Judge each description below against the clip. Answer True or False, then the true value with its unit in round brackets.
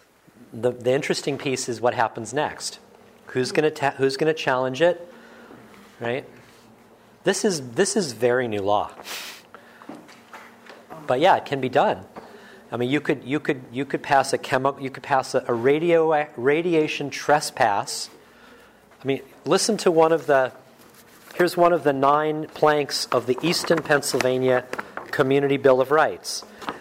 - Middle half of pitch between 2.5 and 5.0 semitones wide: True (4.0 semitones)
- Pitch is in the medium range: True (145 Hz)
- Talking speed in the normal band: True (150 wpm)